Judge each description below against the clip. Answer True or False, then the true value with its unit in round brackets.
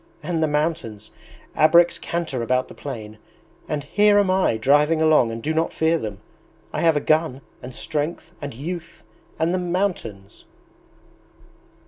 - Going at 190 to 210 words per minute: False (150 wpm)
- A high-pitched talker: False (155 Hz)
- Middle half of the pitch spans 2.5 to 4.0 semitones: False (4.9 semitones)